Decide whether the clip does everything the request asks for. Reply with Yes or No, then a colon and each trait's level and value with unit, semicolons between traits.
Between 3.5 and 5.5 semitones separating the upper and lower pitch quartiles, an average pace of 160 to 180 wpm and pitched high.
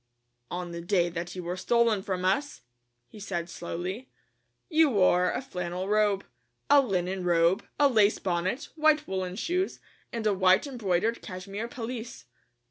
No: average, 4.7 semitones; average, 150 wpm; high, 195 Hz